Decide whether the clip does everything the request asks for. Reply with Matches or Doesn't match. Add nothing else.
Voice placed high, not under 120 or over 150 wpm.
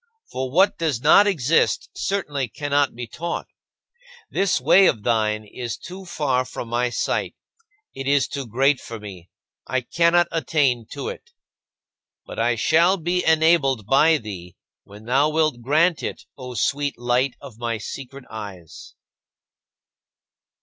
Doesn't match